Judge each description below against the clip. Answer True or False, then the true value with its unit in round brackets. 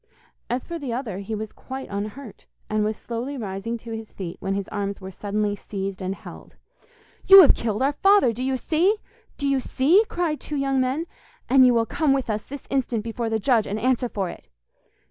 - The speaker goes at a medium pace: False (210 wpm)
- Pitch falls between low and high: False (235 Hz)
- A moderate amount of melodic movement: True (4.6 semitones)